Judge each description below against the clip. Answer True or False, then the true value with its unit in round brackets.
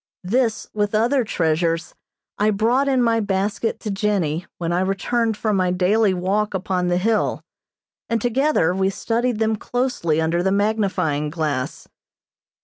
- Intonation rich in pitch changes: False (4.0 semitones)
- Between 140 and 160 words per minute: True (145 wpm)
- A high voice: True (200 Hz)